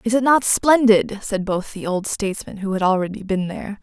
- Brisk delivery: Yes, fast, 220 wpm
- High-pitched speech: Yes, high, 205 Hz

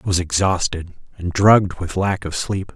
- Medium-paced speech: Yes, average, 195 wpm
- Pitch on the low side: Yes, very low, 90 Hz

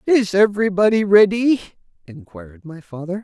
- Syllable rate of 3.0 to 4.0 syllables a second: No, 5.0 syllables/s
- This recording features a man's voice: Yes, male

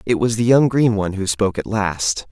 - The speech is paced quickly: Yes, fast, 260 wpm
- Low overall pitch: Yes, low, 105 Hz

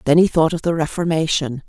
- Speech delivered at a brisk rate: Yes, fast, 215 wpm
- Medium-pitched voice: Yes, medium, 160 Hz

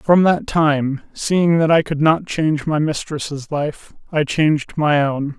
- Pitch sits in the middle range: Yes, medium, 150 Hz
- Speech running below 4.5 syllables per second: Yes, 3.7 syllables/s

